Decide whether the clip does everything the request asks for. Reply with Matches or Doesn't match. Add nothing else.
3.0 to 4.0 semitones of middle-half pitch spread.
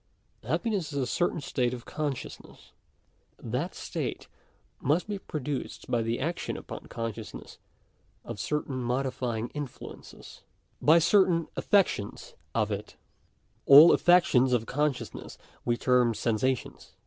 Doesn't match